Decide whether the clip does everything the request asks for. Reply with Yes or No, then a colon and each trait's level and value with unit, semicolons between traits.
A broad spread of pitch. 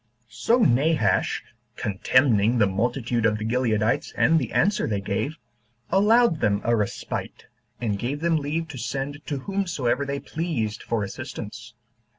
Yes: wide, 6.1 semitones